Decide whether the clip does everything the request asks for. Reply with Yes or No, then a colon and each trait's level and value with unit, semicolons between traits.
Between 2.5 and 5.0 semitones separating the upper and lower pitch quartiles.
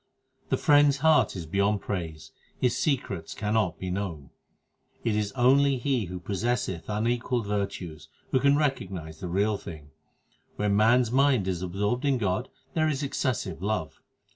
No: wide, 5.6 semitones